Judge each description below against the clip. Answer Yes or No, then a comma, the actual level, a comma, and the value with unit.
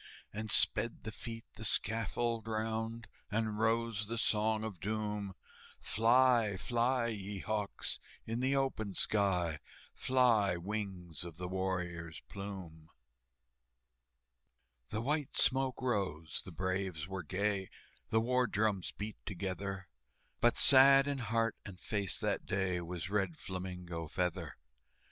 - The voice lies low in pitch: Yes, low, 105 Hz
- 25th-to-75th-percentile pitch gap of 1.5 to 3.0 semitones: No, average, 3.5 semitones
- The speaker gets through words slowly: Yes, slow, 125 wpm